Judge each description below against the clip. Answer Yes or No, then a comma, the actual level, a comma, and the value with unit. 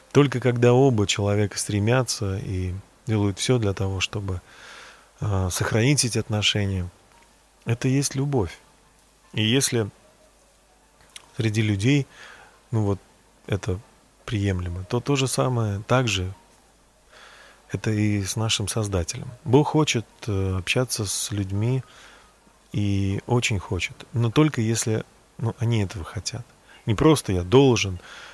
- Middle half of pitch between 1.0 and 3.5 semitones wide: No, average, 4.2 semitones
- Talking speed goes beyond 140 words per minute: No, average, 115 wpm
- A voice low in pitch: Yes, low, 110 Hz